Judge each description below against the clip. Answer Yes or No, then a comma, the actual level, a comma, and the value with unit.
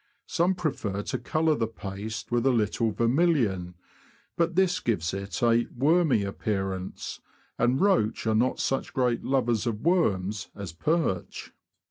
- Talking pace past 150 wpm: No, average, 145 wpm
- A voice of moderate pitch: No, low, 115 Hz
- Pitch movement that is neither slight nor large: No, wide, 7.0 semitones